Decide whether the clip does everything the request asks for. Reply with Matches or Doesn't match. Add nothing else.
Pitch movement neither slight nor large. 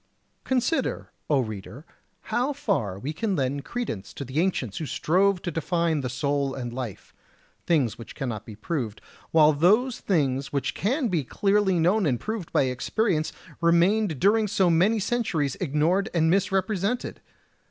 Doesn't match